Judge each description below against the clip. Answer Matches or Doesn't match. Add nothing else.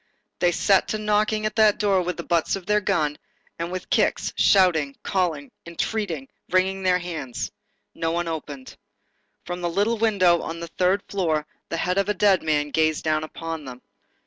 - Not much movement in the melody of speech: Doesn't match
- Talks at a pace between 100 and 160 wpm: Doesn't match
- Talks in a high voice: Doesn't match